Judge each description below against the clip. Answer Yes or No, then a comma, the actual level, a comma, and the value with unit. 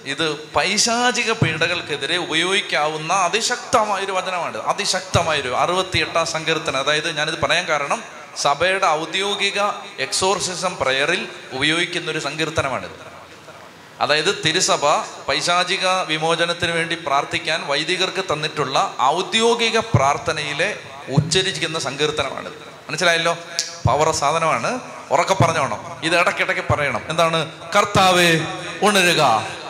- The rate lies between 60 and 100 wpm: Yes, average, 90 wpm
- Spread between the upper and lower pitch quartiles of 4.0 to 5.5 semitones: No, average, 3.5 semitones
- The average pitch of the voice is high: No, medium, 165 Hz